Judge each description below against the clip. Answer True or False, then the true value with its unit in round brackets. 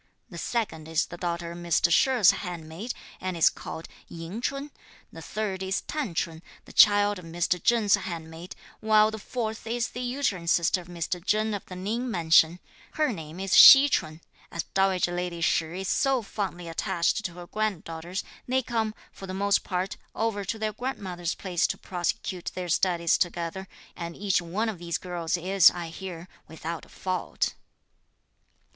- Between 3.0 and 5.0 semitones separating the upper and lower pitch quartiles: True (4.0 semitones)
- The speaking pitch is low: False (185 Hz)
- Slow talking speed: False (175 wpm)